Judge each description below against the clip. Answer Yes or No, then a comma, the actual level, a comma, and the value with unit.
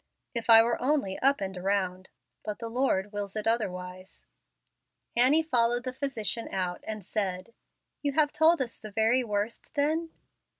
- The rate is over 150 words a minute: Yes, average, 160 wpm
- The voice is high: Yes, high, 225 Hz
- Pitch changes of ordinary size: Yes, average, 4.8 semitones